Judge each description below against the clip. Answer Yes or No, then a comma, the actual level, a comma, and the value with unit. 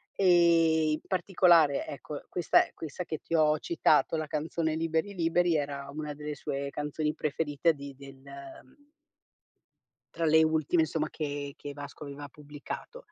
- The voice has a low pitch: No, medium, 155 Hz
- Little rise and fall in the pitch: Yes, narrow, 2.3 semitones